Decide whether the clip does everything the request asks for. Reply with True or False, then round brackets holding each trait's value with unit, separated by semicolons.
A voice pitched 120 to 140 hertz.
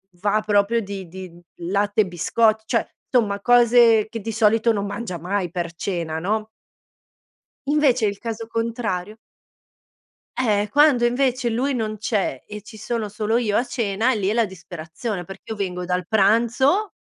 False (215 Hz)